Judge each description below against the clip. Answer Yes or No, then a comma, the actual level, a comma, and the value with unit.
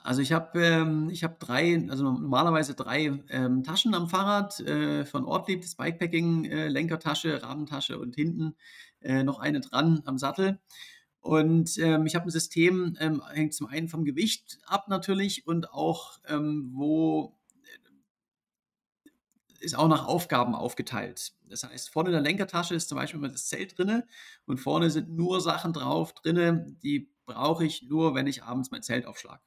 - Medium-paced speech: Yes, average, 170 wpm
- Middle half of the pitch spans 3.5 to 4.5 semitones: No, average, 3.1 semitones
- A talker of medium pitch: Yes, medium, 160 Hz